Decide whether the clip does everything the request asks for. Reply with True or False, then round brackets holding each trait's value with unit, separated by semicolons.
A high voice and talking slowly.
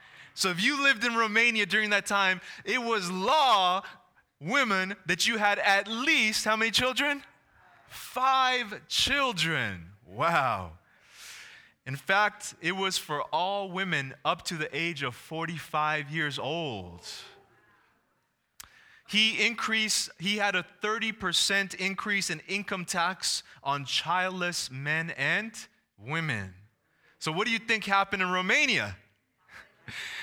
True (195 Hz; 125 wpm)